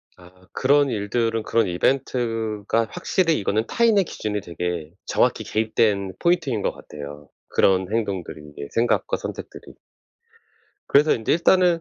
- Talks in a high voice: No, low, 110 Hz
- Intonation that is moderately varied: No, wide, 6.1 semitones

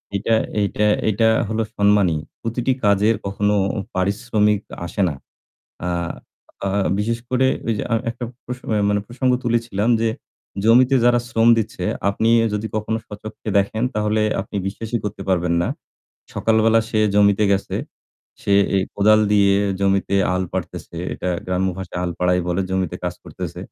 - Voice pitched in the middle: No, low, 105 Hz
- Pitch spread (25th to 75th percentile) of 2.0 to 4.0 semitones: Yes, narrow, 2.5 semitones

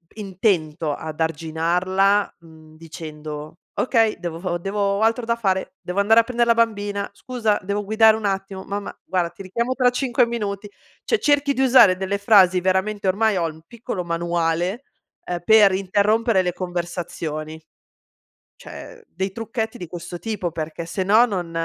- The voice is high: Yes, high, 195 Hz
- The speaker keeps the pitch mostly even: No, average, 4.3 semitones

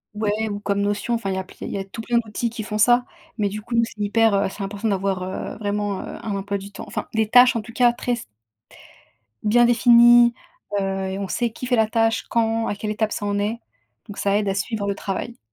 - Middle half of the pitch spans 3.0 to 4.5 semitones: No, narrow, 2.6 semitones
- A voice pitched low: No, high, 215 Hz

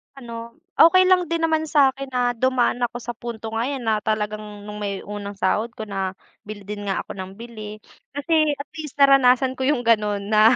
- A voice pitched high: Yes, high, 235 Hz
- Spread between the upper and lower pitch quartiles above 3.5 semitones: Yes, average, 4.6 semitones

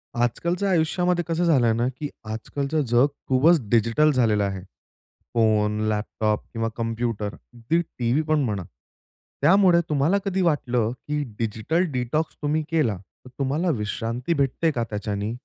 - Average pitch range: No, wide, 6.0 semitones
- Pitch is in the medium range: No, low, 125 Hz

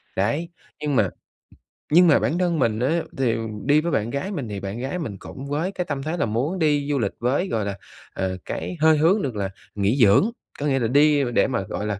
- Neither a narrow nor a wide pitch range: No, wide, 6.3 semitones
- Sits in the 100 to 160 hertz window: Yes, medium, 140 Hz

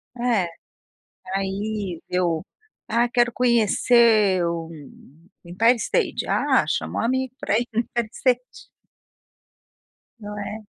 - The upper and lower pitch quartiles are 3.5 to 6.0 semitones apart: Yes, average, 3.8 semitones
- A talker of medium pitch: No, high, 220 Hz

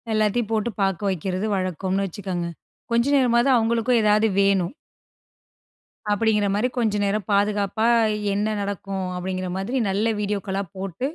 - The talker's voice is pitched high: Yes, high, 205 Hz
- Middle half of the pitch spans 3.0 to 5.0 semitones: No, narrow, 2.5 semitones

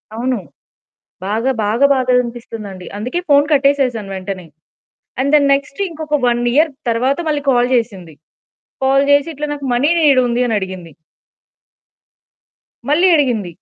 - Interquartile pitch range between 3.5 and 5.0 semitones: Yes, average, 4.2 semitones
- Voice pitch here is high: Yes, very high, 250 Hz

